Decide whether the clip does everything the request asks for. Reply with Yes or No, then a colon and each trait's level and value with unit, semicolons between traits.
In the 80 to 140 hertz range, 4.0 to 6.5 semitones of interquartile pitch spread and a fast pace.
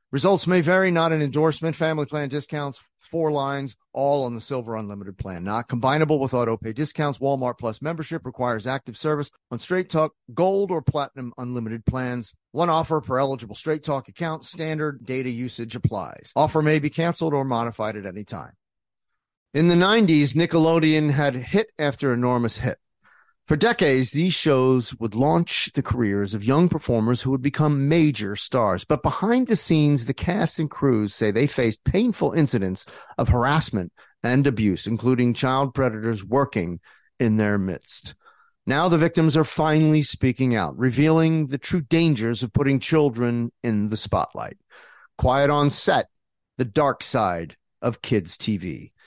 No: low, 135 Hz; average, 4.7 semitones; average, 160 wpm